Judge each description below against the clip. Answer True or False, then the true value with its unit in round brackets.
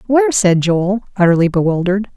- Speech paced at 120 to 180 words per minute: True (140 wpm)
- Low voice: False (185 Hz)